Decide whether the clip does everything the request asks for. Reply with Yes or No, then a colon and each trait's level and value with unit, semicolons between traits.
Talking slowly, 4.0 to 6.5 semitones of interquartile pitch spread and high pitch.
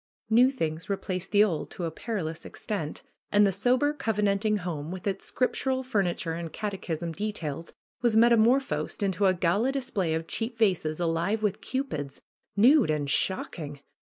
No: average, 155 wpm; average, 5.3 semitones; high, 195 Hz